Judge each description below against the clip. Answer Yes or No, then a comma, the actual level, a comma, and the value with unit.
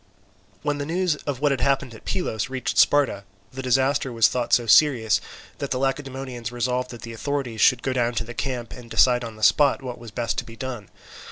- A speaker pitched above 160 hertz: No, low, 125 Hz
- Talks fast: Yes, fast, 215 wpm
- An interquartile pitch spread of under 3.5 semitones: Yes, average, 2.7 semitones